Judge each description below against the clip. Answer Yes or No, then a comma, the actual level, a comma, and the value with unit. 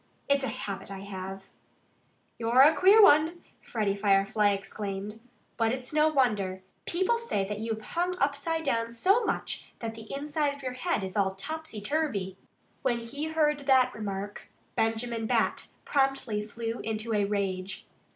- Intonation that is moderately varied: No, wide, 6.2 semitones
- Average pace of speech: Yes, average, 155 wpm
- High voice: Yes, high, 230 Hz